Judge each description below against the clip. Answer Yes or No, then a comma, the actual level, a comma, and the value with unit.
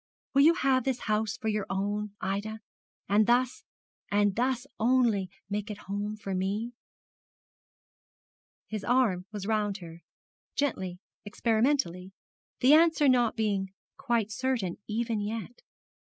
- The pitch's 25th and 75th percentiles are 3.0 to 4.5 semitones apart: Yes, average, 3.5 semitones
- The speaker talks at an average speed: No, slow, 130 wpm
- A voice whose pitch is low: No, high, 215 Hz